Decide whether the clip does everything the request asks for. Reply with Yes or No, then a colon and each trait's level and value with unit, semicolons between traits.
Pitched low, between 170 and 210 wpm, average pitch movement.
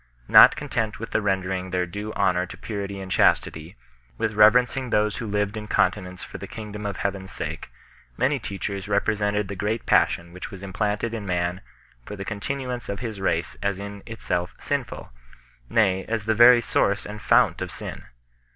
No: low, 100 Hz; average, 185 wpm; narrow, 2.3 semitones